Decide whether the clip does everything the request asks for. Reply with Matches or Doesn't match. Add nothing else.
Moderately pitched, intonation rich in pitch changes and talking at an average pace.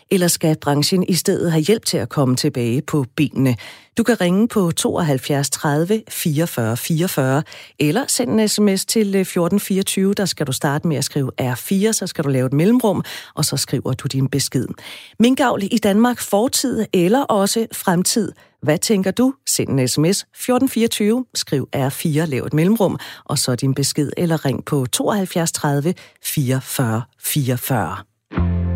Matches